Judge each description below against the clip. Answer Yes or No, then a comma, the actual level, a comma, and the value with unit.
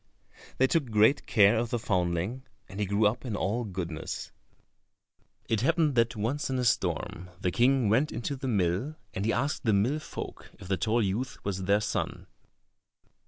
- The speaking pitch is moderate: No, low, 110 Hz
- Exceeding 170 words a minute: Yes, average, 180 wpm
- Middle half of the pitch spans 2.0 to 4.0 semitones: No, average, 4.5 semitones